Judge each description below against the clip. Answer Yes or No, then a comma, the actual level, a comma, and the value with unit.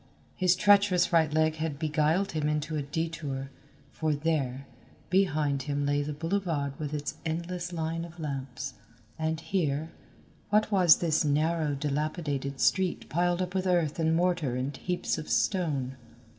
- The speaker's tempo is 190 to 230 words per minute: No, average, 150 wpm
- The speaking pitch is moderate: Yes, medium, 160 Hz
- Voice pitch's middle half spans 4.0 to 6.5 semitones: No, average, 3.3 semitones